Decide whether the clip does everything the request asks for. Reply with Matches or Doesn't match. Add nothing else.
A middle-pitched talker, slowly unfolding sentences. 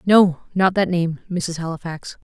Matches